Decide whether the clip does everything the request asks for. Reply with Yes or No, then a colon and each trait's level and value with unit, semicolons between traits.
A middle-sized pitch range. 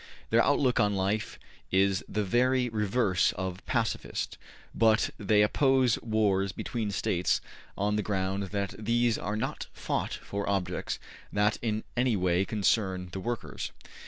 Yes: average, 3.0 semitones